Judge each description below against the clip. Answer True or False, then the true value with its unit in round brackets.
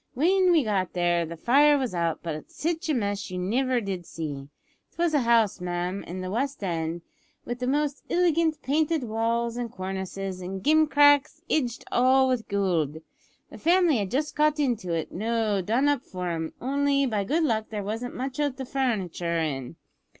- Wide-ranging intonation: True (7.5 semitones)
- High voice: True (230 Hz)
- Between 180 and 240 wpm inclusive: True (185 wpm)